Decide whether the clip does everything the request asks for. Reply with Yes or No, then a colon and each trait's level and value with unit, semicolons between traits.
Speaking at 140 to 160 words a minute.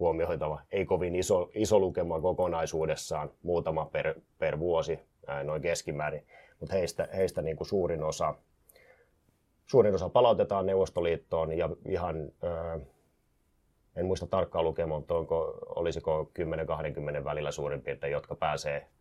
No: average, 125 wpm